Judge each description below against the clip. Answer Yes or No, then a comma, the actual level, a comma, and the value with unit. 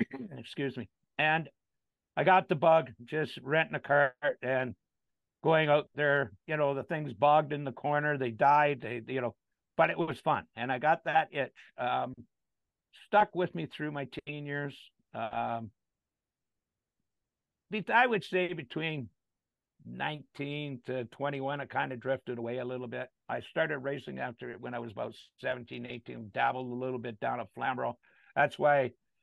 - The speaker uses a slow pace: No, average, 170 wpm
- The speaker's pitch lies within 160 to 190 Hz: No, medium, 140 Hz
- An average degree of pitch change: Yes, average, 3.5 semitones